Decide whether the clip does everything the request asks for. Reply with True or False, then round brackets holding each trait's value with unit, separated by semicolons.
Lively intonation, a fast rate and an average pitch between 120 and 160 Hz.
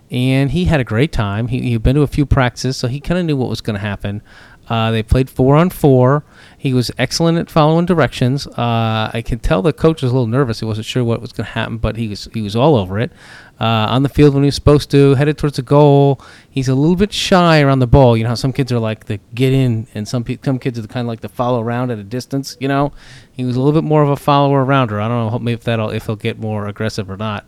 False (3.7 semitones; 285 wpm; 125 Hz)